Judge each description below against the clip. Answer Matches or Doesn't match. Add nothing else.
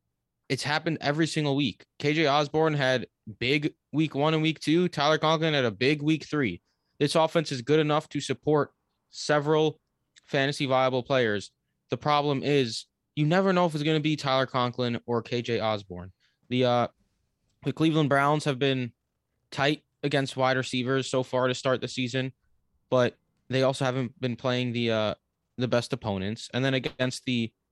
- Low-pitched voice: Matches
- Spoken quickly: Doesn't match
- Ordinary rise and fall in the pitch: Matches